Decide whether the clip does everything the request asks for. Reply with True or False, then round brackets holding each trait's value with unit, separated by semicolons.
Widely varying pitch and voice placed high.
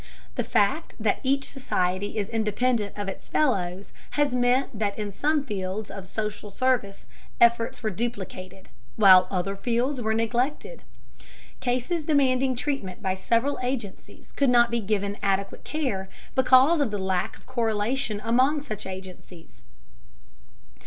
False (4.6 semitones; 225 Hz)